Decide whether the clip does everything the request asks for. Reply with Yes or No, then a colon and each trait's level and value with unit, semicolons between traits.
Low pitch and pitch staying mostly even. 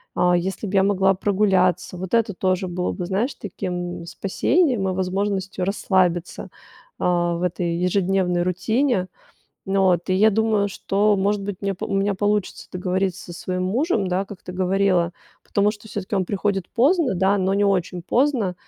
No: high, 190 Hz; narrow, 2.1 semitones